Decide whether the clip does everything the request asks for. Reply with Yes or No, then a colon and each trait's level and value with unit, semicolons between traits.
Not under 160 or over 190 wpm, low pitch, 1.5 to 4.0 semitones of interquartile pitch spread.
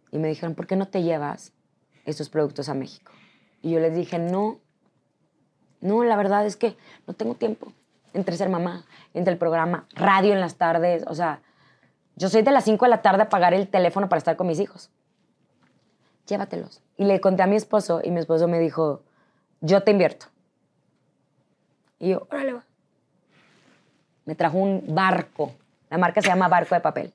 No: average, 185 wpm; medium, 180 Hz; average, 3.3 semitones